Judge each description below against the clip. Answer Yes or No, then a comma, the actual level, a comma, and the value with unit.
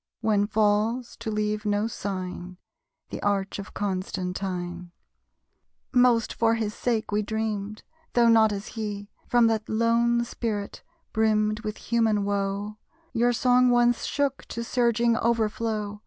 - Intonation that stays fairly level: Yes, narrow, 2.2 semitones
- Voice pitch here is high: Yes, high, 215 Hz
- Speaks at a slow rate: Yes, slow, 130 wpm